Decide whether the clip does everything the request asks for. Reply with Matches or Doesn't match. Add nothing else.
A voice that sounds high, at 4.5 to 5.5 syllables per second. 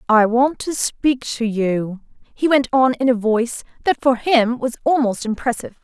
Matches